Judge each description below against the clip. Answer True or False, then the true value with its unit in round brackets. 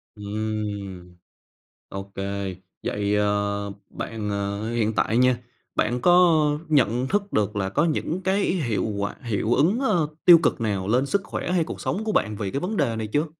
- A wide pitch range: True (6.6 semitones)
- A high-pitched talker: False (110 Hz)